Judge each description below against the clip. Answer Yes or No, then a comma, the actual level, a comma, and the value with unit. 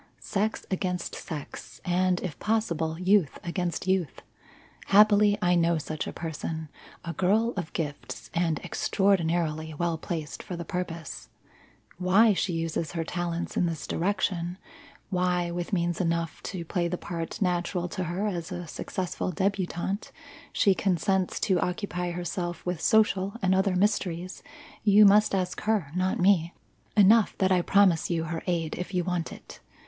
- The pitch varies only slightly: Yes, narrow, 2.3 semitones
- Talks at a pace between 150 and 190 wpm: Yes, average, 155 wpm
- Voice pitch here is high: No, medium, 180 Hz